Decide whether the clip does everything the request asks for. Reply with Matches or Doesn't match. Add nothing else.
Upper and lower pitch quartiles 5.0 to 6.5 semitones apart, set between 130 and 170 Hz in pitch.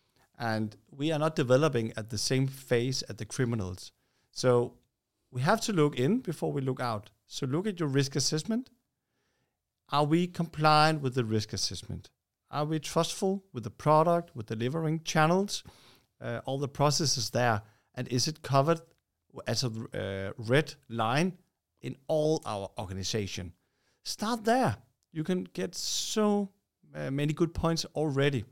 Matches